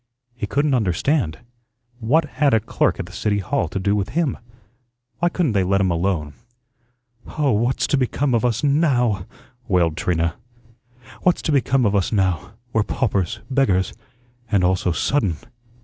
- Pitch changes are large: Yes, wide, 6.6 semitones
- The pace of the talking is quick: No, average, 165 wpm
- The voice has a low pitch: Yes, low, 105 Hz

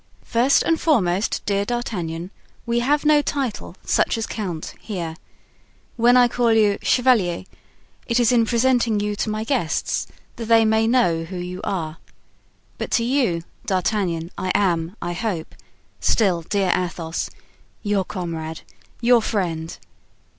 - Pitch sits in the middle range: No, high, 210 Hz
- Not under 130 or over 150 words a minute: Yes, average, 140 wpm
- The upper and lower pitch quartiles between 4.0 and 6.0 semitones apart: Yes, average, 5.3 semitones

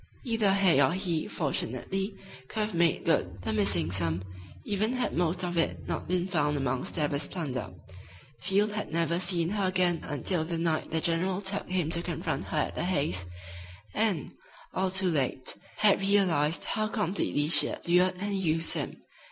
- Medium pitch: Yes, medium, 170 Hz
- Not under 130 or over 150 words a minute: No, average, 175 wpm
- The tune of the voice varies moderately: Yes, average, 4.5 semitones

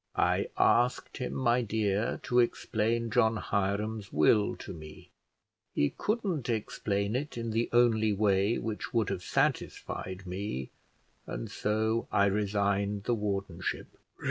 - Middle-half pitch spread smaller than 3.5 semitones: Yes, average, 2.7 semitones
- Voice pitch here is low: Yes, low, 105 Hz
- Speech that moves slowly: Yes, slow, 130 wpm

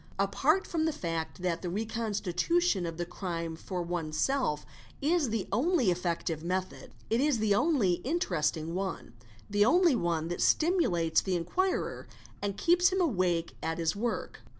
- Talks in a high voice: Yes, high, 195 Hz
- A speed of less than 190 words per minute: Yes, average, 150 wpm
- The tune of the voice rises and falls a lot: Yes, wide, 8.4 semitones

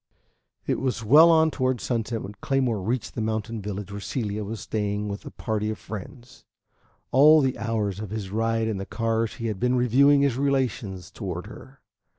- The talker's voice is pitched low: Yes, low, 115 Hz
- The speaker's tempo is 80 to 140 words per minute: No, average, 190 wpm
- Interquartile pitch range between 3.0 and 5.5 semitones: Yes, average, 3.7 semitones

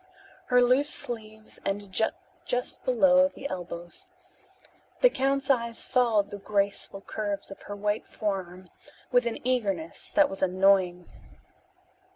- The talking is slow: Yes, slow, 125 wpm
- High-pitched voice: Yes, high, 210 Hz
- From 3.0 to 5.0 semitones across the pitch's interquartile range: Yes, average, 4.3 semitones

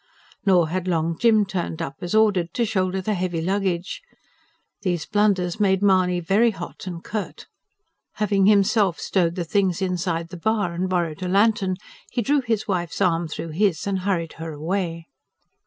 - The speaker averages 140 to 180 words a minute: Yes, average, 170 wpm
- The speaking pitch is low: No, medium, 185 Hz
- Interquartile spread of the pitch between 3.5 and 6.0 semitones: No, average, 3.0 semitones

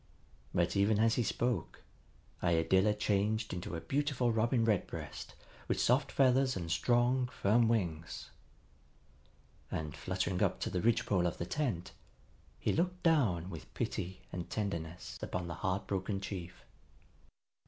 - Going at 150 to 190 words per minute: No, slow, 135 wpm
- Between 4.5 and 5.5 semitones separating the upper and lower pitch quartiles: Yes, average, 5.2 semitones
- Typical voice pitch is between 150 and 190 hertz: No, low, 100 Hz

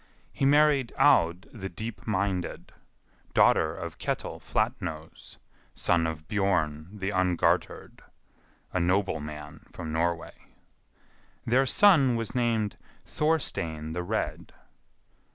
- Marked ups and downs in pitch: Yes, wide, 5.9 semitones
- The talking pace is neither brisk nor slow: No, slow, 105 wpm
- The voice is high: No, very low, 95 Hz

